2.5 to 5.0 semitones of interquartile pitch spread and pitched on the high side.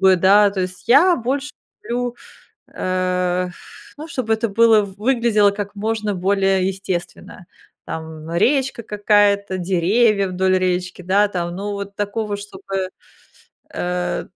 Yes: average, 2.9 semitones; high, 200 Hz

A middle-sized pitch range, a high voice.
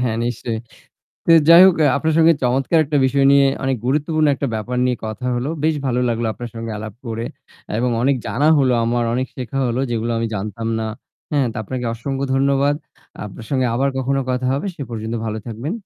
No: average, 3.2 semitones; low, 125 Hz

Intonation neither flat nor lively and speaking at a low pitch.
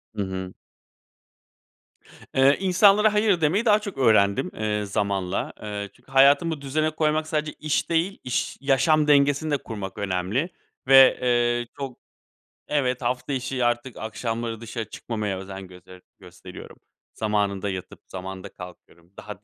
No: wide, 6.8 semitones; low, 120 Hz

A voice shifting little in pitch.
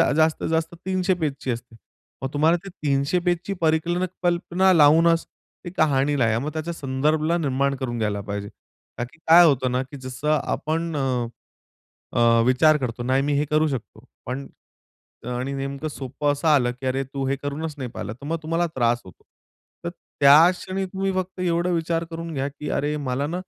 No: average, 4.0 semitones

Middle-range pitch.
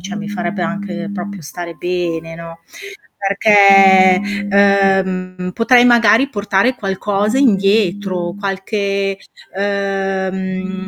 No: high, 195 Hz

